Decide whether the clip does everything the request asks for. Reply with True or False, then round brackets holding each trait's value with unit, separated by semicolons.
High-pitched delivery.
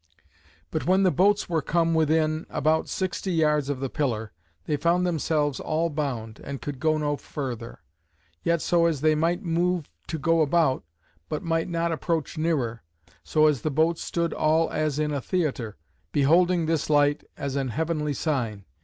False (155 Hz)